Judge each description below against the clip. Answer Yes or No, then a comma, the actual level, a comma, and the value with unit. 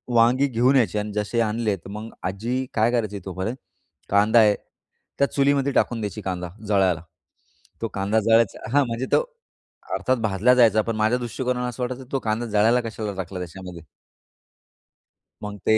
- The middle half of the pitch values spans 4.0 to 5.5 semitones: No, average, 3.3 semitones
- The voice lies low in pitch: Yes, low, 110 Hz